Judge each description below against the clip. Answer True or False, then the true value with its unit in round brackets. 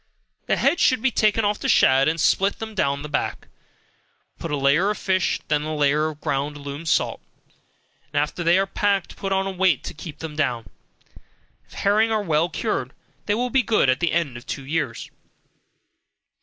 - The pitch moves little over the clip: False (5.6 semitones)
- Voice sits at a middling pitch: True (165 Hz)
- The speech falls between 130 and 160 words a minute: False (195 wpm)